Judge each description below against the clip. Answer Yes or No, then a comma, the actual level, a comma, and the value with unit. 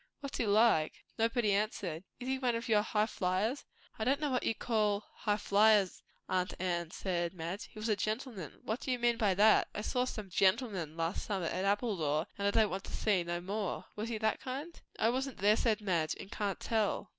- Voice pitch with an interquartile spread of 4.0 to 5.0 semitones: No, average, 3.6 semitones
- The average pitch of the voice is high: Yes, high, 210 Hz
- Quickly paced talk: Yes, fast, 215 wpm